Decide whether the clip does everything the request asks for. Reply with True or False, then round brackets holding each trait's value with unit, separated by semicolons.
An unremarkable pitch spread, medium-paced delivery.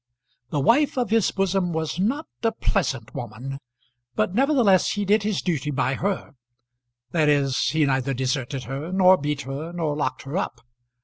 False (6.4 semitones; 170 wpm)